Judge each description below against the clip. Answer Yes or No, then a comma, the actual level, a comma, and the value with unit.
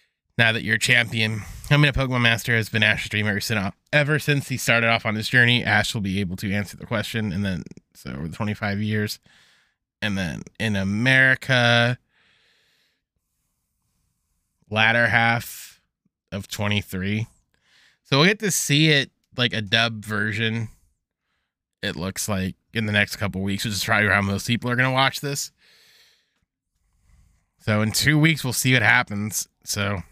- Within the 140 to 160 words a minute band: No, average, 170 wpm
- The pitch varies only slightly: No, average, 3.2 semitones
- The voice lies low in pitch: Yes, low, 110 Hz